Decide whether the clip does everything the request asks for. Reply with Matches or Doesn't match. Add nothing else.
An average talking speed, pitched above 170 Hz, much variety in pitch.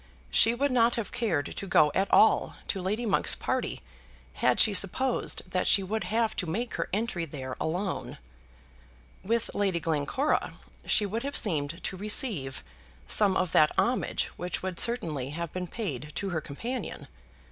Matches